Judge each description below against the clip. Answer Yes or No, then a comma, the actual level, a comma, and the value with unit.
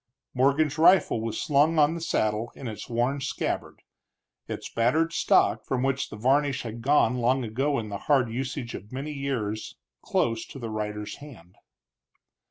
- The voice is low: Yes, low, 130 Hz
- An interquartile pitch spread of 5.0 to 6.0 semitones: No, average, 4.1 semitones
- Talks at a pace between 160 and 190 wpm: Yes, average, 165 wpm